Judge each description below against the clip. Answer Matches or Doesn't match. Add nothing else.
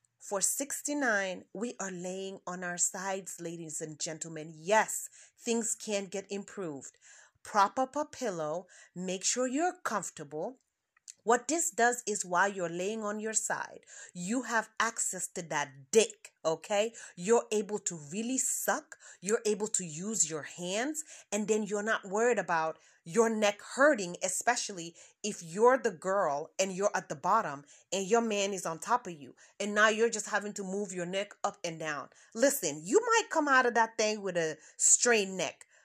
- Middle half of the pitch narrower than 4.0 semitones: Doesn't match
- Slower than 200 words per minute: Matches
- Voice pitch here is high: Matches